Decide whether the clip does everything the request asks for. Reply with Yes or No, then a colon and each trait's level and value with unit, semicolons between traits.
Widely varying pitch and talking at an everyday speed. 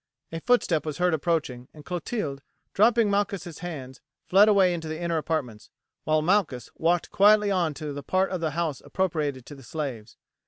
No: average, 4.4 semitones; average, 180 wpm